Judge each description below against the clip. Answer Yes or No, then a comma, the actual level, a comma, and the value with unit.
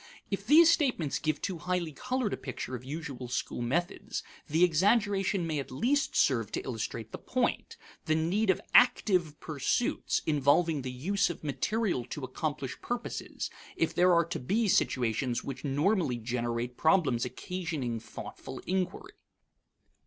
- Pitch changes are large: Yes, wide, 6.8 semitones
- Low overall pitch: No, medium, 160 Hz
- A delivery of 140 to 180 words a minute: Yes, average, 145 wpm